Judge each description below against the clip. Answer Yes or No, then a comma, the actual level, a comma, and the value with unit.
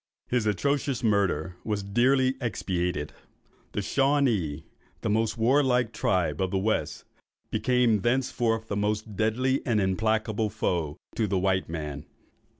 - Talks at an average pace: No, slow, 130 wpm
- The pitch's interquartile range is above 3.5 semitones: Yes, average, 4.4 semitones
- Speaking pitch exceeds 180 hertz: No, low, 110 Hz